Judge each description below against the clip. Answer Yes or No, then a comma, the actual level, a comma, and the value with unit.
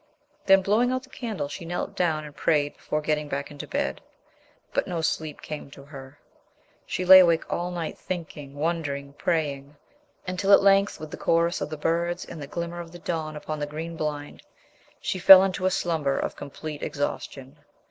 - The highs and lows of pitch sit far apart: No, average, 3.3 semitones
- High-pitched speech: No, medium, 160 Hz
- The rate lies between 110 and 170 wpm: No, average, 190 wpm